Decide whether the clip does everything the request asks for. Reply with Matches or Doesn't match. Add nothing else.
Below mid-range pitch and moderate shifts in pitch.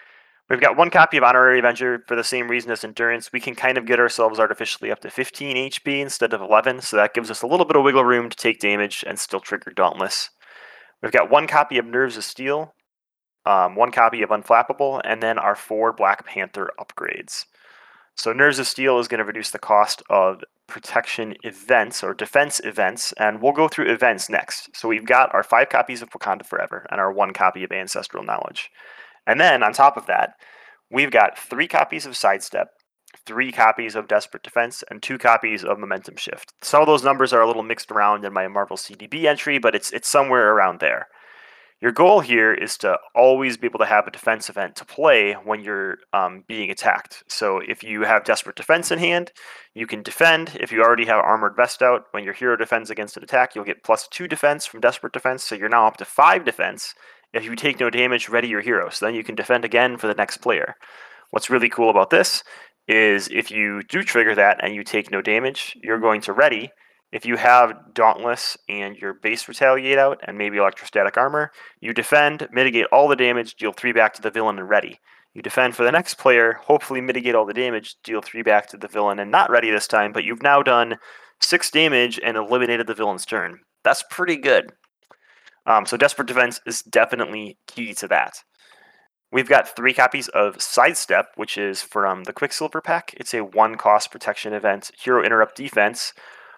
Matches